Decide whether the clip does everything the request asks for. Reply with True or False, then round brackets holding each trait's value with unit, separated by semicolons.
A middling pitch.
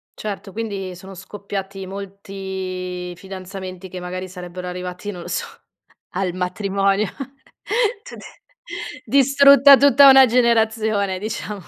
False (195 Hz)